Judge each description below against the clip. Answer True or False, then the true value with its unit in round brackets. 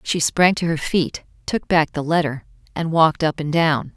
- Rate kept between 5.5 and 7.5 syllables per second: False (4.8 syllables/s)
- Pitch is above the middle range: False (160 Hz)